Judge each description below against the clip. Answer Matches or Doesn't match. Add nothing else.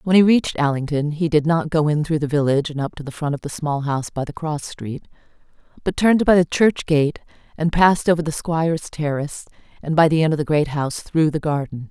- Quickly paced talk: Matches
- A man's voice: Doesn't match